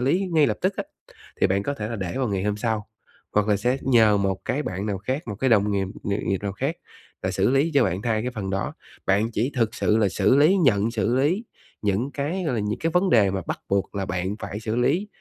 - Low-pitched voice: Yes, low, 110 Hz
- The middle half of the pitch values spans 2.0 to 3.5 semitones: No, average, 5.1 semitones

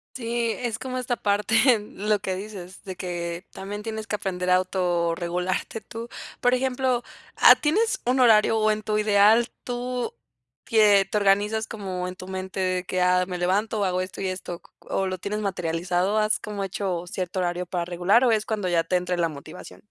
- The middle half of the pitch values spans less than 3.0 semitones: No, average, 3.3 semitones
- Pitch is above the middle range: Yes, high, 195 Hz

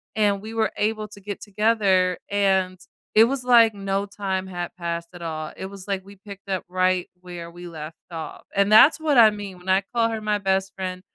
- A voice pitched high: Yes, high, 195 Hz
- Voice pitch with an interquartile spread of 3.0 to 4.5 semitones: No, narrow, 2.5 semitones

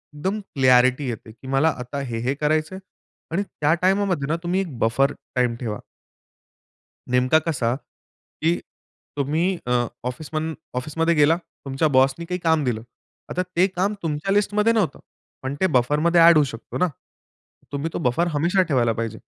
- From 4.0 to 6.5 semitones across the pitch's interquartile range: Yes, average, 5.0 semitones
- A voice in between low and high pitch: Yes, medium, 150 Hz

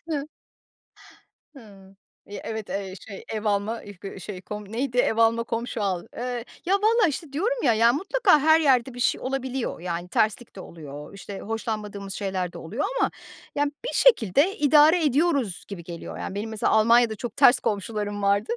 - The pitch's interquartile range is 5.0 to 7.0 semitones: Yes, wide, 5.5 semitones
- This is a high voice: Yes, high, 225 Hz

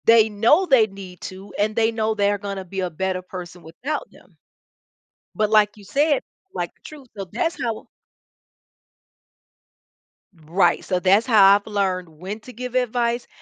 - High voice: Yes, high, 210 Hz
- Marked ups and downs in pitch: No, average, 3.7 semitones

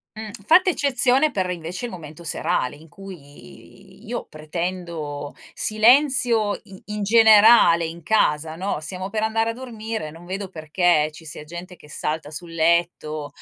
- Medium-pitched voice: Yes, medium, 180 Hz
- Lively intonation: Yes, wide, 5.7 semitones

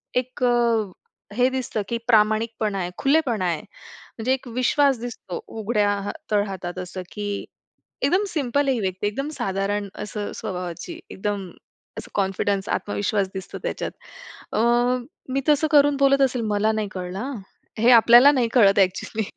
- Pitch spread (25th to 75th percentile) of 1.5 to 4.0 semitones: No, average, 4.5 semitones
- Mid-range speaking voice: No, high, 215 Hz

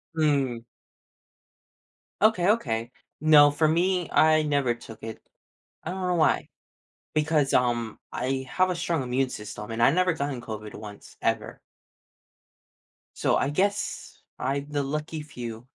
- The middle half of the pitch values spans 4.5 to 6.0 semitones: Yes, average, 4.9 semitones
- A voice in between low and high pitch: Yes, medium, 145 Hz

